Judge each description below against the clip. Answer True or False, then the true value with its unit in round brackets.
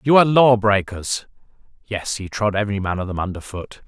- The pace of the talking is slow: False (200 wpm)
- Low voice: True (105 Hz)